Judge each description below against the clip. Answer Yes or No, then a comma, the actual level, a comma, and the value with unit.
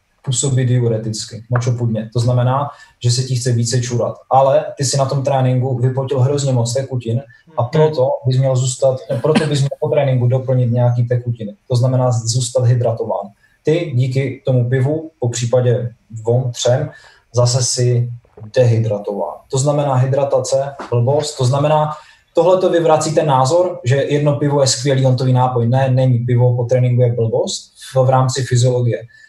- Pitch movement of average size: No, narrow, 2.1 semitones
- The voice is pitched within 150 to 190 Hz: No, low, 130 Hz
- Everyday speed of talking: Yes, average, 160 wpm